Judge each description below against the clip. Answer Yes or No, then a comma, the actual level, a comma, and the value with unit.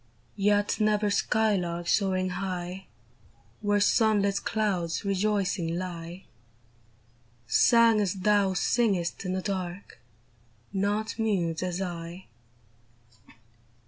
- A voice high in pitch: Yes, high, 195 Hz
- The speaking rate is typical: No, slow, 95 wpm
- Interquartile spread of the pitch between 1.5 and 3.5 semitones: Yes, average, 2.7 semitones